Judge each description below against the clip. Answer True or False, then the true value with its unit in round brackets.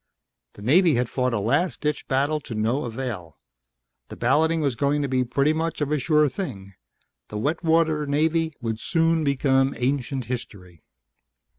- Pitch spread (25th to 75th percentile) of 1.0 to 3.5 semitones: False (4.3 semitones)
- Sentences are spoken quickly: False (165 wpm)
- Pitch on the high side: False (140 Hz)